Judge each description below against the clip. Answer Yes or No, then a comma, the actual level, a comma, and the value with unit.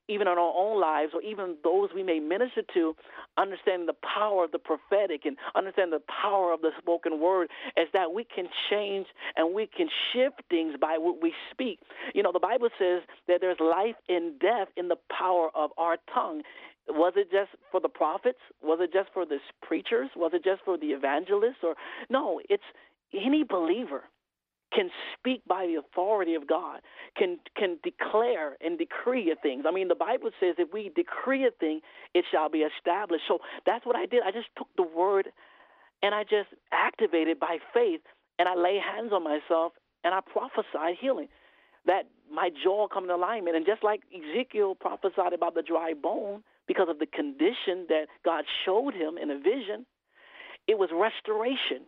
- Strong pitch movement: Yes, wide, 7.3 semitones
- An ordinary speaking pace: Yes, average, 185 wpm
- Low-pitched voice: No, high, 195 Hz